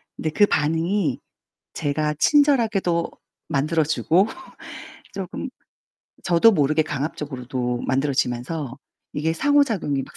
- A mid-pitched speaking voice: Yes, medium, 155 Hz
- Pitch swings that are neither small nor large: Yes, average, 4.5 semitones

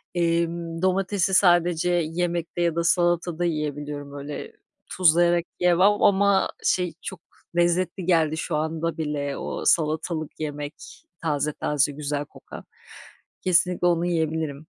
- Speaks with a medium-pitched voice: Yes, medium, 170 Hz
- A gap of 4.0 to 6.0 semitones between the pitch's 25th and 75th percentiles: No, narrow, 2.5 semitones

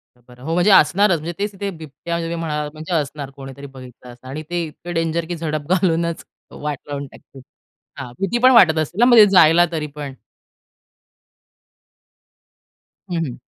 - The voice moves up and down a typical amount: Yes, average, 3.5 semitones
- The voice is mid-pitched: Yes, medium, 160 Hz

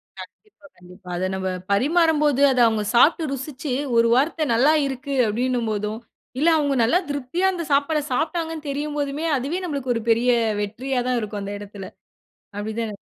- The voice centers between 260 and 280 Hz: Yes, very high, 265 Hz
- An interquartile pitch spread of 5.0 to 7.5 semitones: Yes, wide, 5.4 semitones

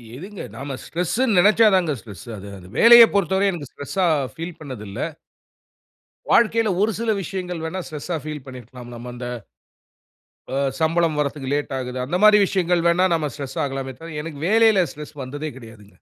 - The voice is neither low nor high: Yes, medium, 160 Hz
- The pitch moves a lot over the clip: Yes, wide, 6.1 semitones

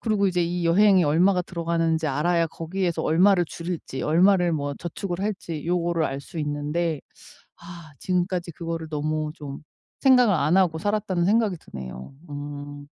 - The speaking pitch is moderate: Yes, medium, 170 Hz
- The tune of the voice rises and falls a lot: No, average, 2.9 semitones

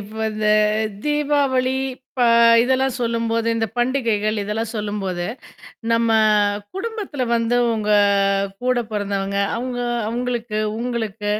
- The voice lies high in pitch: Yes, high, 230 Hz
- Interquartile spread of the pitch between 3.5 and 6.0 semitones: No, average, 3.0 semitones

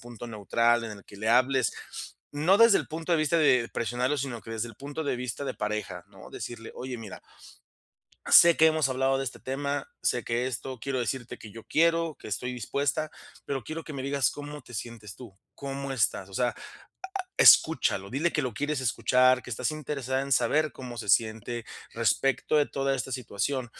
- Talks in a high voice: No, low, 130 Hz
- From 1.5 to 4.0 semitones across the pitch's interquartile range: Yes, average, 3.5 semitones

